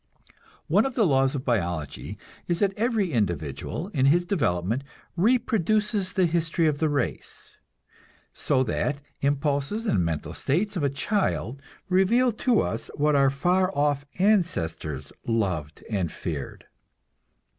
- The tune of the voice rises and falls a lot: Yes, wide, 8.7 semitones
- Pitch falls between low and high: Yes, medium, 150 Hz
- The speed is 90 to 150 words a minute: Yes, slow, 135 wpm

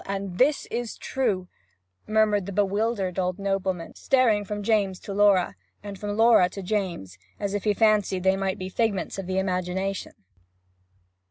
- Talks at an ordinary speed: Yes, average, 160 wpm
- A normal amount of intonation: No, narrow, 2.1 semitones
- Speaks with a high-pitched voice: Yes, high, 195 Hz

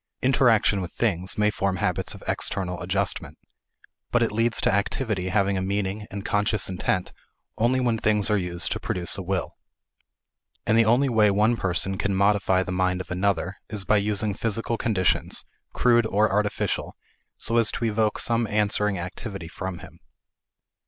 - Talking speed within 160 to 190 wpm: Yes, average, 165 wpm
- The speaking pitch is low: Yes, low, 100 Hz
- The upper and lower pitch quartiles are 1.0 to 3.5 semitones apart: Yes, average, 2.8 semitones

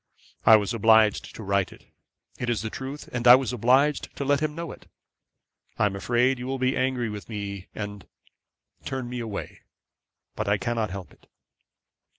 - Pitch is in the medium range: No, low, 120 Hz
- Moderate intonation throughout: Yes, average, 3.9 semitones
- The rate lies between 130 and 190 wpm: Yes, average, 180 wpm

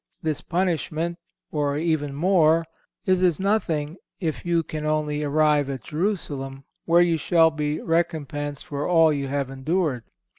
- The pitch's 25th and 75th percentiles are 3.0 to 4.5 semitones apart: No, narrow, 2.6 semitones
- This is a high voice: No, medium, 155 Hz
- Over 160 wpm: No, average, 145 wpm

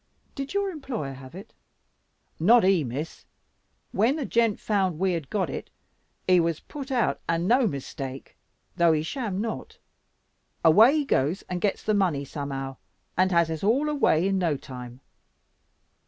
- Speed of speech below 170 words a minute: Yes, average, 160 wpm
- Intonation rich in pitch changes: Yes, wide, 7.1 semitones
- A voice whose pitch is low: No, medium, 185 Hz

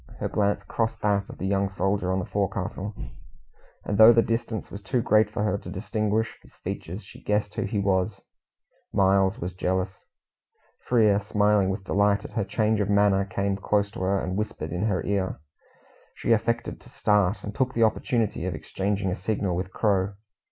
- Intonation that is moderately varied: No, narrow, 1.9 semitones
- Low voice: Yes, low, 100 Hz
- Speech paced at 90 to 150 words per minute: No, average, 190 wpm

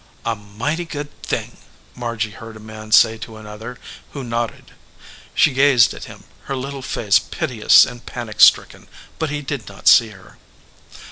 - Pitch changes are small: No, average, 4.0 semitones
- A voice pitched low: Yes, low, 115 Hz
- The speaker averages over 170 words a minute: No, average, 160 wpm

